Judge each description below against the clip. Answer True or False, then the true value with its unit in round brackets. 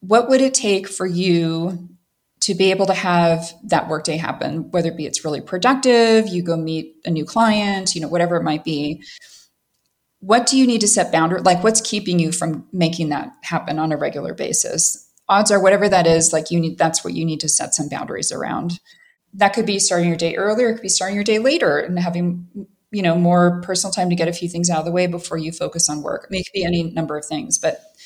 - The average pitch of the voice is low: False (175 Hz)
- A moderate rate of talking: False (240 wpm)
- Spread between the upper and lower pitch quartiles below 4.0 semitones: True (3.5 semitones)